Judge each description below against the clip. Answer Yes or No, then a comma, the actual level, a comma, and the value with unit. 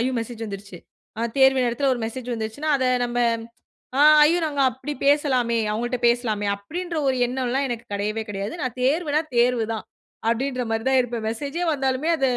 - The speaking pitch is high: Yes, very high, 250 Hz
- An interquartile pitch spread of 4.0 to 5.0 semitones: No, average, 3.4 semitones